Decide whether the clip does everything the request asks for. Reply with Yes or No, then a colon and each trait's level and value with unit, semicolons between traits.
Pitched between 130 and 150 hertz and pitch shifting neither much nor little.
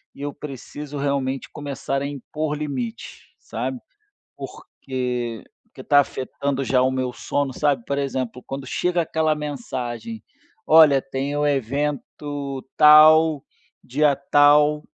No: medium, 140 Hz; narrow, 2.1 semitones